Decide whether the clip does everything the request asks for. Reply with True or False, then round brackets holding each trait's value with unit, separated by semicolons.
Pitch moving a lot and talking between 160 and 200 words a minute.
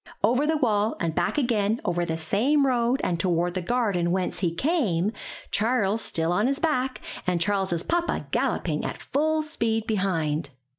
True (6.6 semitones; 165 wpm)